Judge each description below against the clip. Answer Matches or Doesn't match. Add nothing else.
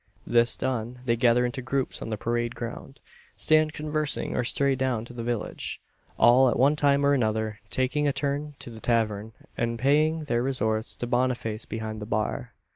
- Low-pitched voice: Matches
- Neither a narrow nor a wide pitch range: Matches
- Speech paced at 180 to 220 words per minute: Matches